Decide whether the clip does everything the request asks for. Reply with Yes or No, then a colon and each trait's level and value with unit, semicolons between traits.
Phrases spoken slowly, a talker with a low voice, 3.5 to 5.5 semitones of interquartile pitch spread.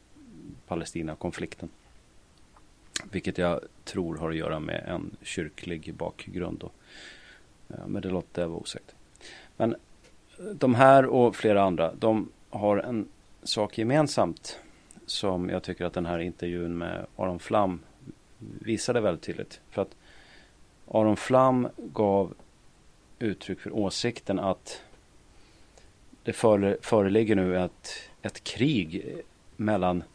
Yes: slow, 115 wpm; low, 100 Hz; average, 4.0 semitones